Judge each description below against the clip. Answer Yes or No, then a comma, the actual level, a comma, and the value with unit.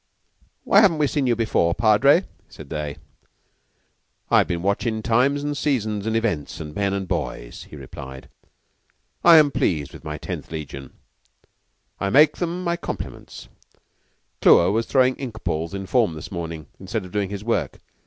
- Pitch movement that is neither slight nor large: No, wide, 8.0 semitones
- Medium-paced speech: Yes, average, 165 wpm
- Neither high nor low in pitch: No, low, 105 Hz